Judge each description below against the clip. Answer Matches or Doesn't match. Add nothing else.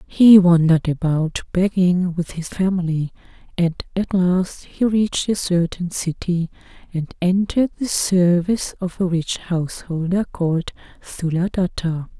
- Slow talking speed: Matches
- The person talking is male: Doesn't match